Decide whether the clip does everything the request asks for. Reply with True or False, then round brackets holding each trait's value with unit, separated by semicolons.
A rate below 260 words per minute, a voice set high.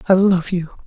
False (210 wpm; 180 Hz)